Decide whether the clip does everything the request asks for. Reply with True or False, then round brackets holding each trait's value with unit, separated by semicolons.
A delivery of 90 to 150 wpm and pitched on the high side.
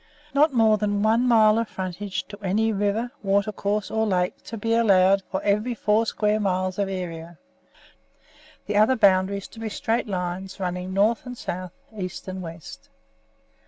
False (160 wpm; 205 Hz)